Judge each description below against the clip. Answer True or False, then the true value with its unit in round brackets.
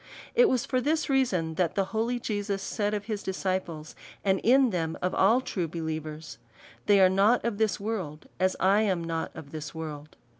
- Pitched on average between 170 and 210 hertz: True (190 Hz)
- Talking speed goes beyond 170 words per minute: True (195 wpm)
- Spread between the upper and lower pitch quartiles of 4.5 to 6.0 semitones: True (5.3 semitones)